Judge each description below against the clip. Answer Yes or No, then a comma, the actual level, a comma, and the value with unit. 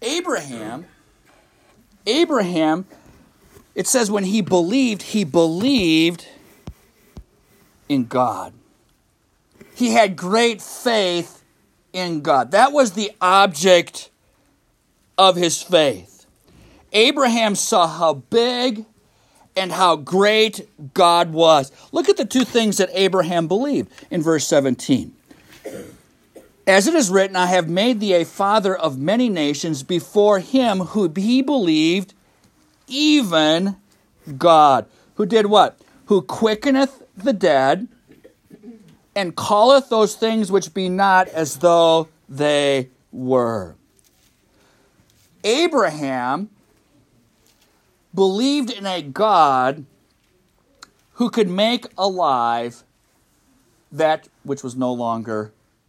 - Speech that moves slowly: Yes, slow, 105 wpm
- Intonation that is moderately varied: No, wide, 5.9 semitones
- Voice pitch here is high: Yes, high, 195 Hz